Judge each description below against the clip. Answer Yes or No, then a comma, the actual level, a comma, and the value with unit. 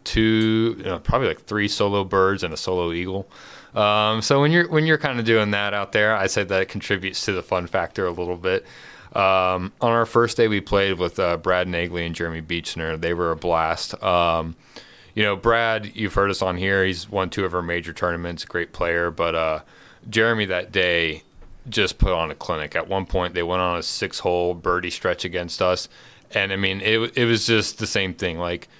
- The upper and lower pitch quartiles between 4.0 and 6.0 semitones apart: No, average, 3.3 semitones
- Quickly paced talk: Yes, fast, 220 wpm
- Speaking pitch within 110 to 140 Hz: No, very low, 95 Hz